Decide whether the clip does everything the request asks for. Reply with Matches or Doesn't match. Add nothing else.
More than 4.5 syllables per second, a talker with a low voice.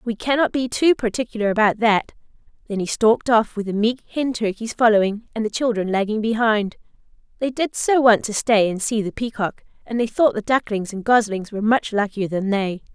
Doesn't match